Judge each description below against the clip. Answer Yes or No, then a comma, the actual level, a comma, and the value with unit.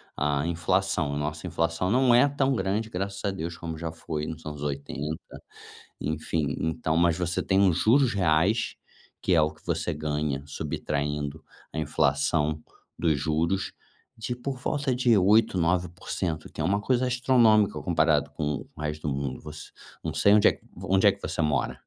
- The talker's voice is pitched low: Yes, very low, 85 Hz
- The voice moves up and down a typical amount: Yes, average, 4.8 semitones